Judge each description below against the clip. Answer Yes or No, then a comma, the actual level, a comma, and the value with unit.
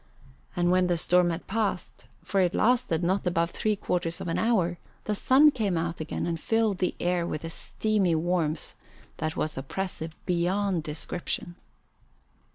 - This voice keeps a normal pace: Yes, average, 165 wpm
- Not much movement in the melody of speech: No, average, 3.1 semitones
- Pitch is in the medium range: Yes, medium, 175 Hz